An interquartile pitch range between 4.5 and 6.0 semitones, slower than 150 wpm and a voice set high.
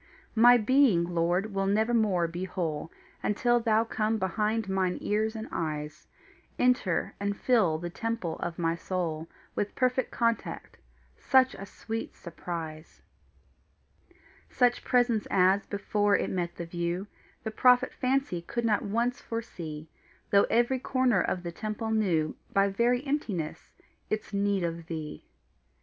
Yes: average, 5.0 semitones; slow, 135 wpm; high, 200 Hz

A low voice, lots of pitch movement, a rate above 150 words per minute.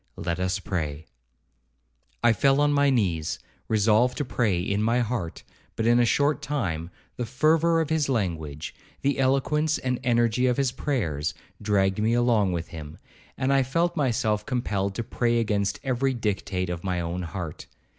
Yes: low, 115 Hz; wide, 6.1 semitones; average, 165 wpm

